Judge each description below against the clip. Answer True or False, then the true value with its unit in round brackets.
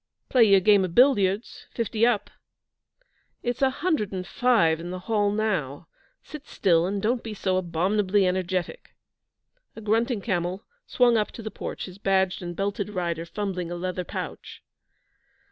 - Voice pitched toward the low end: False (195 Hz)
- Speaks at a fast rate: False (160 wpm)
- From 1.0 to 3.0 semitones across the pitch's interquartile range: False (3.5 semitones)